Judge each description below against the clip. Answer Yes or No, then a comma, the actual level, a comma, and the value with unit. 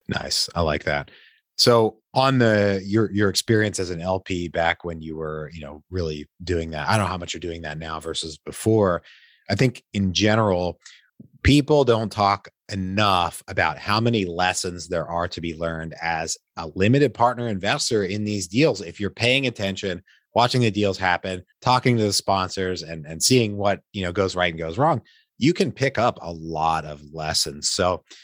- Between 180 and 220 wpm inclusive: Yes, average, 190 wpm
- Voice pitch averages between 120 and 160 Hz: No, very low, 95 Hz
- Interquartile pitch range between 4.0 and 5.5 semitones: Yes, average, 4.4 semitones